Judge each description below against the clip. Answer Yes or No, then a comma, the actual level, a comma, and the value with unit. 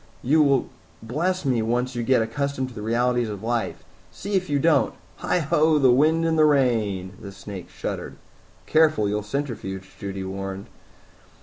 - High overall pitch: No, low, 125 Hz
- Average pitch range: No, wide, 6.2 semitones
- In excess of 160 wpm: Yes, average, 170 wpm